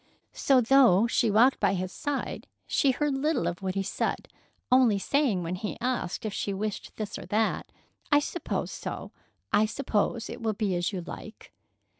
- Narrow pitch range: No, average, 5.0 semitones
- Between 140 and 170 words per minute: No, average, 180 wpm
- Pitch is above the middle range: Yes, high, 220 Hz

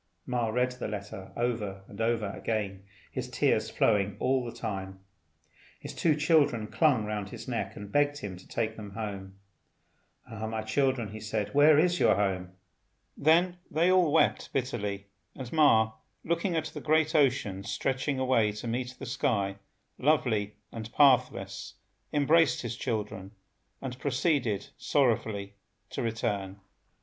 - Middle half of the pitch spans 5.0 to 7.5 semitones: Yes, wide, 5.4 semitones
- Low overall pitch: Yes, low, 115 Hz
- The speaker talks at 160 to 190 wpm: No, average, 145 wpm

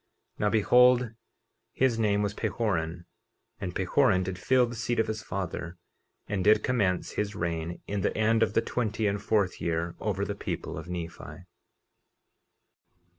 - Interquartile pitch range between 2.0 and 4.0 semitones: Yes, average, 3.7 semitones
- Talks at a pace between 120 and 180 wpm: Yes, average, 160 wpm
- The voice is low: Yes, low, 105 Hz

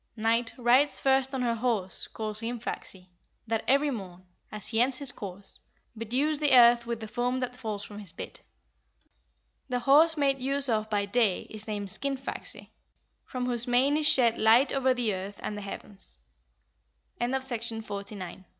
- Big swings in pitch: No, average, 3.7 semitones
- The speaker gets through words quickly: No, average, 180 wpm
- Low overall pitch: No, high, 235 Hz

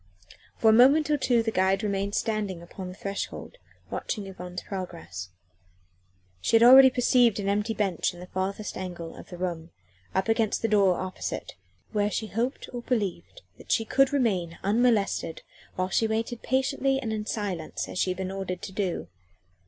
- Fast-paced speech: No, average, 175 wpm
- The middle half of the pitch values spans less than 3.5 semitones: No, average, 3.8 semitones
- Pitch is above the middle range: Yes, high, 205 Hz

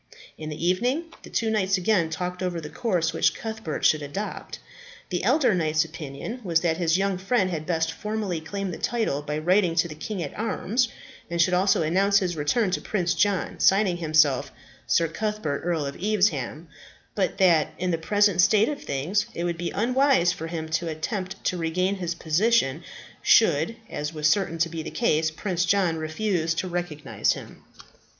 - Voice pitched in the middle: Yes, medium, 175 Hz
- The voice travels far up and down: No, average, 4.0 semitones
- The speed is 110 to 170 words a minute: No, average, 185 wpm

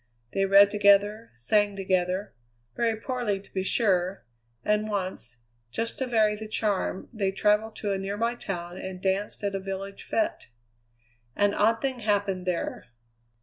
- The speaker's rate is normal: Yes, average, 150 wpm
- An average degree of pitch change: No, narrow, 2.0 semitones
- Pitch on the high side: Yes, high, 200 Hz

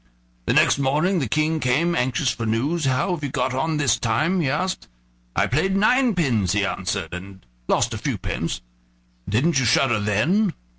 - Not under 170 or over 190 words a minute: Yes, average, 180 wpm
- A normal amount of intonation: No, wide, 6.3 semitones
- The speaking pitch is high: No, medium, 140 Hz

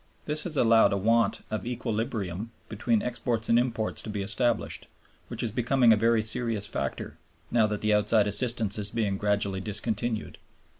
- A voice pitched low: Yes, low, 110 Hz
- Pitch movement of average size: No, narrow, 2.1 semitones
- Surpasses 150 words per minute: Yes, average, 165 wpm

